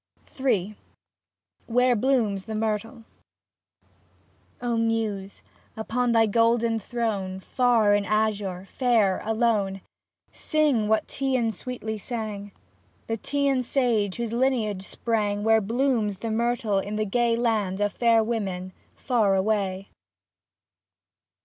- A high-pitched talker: Yes, high, 220 Hz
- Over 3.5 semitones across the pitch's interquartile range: No, average, 2.7 semitones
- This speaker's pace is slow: Yes, slow, 125 wpm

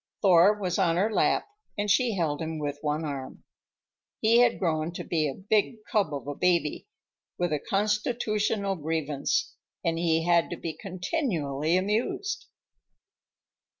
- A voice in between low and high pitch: Yes, medium, 175 Hz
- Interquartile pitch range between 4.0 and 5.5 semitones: Yes, average, 5.0 semitones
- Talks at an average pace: Yes, average, 150 wpm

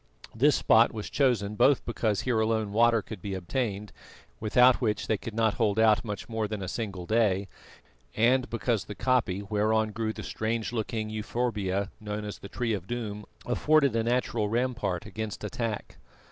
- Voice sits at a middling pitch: No, low, 110 Hz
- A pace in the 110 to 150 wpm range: No, average, 170 wpm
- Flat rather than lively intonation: Yes, narrow, 2.2 semitones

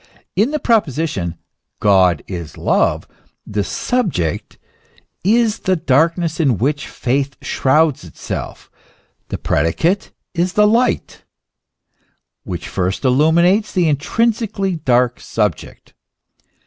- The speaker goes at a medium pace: No, slow, 110 wpm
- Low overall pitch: No, medium, 155 Hz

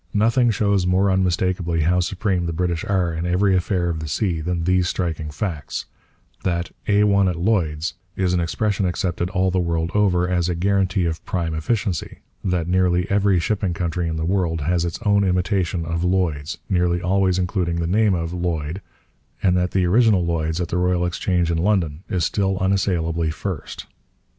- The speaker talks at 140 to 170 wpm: No, average, 180 wpm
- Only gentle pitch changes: Yes, narrow, 2.2 semitones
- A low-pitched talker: Yes, very low, 90 Hz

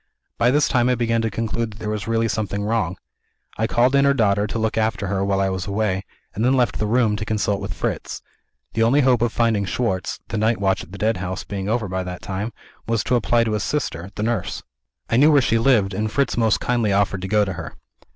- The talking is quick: Yes, fast, 245 wpm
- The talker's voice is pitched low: Yes, low, 110 Hz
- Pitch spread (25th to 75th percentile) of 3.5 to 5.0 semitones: No, average, 2.9 semitones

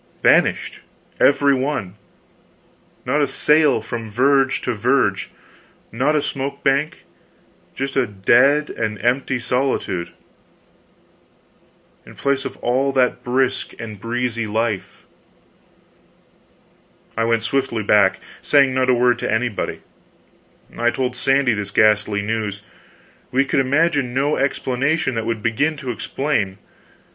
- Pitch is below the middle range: Yes, low, 125 Hz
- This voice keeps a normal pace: No, slow, 120 wpm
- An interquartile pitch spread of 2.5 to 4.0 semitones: Yes, average, 3.5 semitones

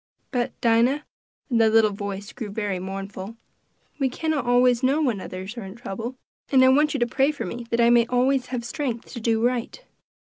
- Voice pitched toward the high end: Yes, high, 235 Hz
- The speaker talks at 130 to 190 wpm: No, fast, 205 wpm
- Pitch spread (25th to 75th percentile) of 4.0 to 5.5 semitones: No, average, 2.9 semitones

